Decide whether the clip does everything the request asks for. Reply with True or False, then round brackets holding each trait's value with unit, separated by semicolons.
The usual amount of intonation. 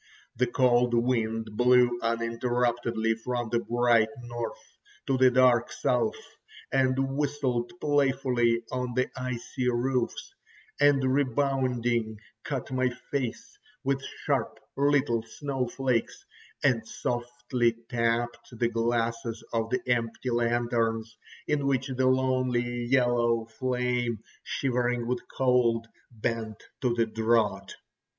False (1.7 semitones)